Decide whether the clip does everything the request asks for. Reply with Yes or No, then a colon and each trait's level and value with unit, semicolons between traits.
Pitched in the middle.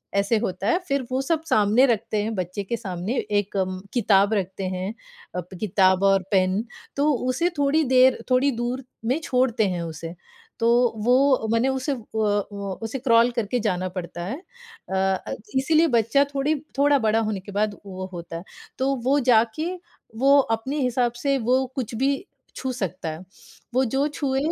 No: high, 230 Hz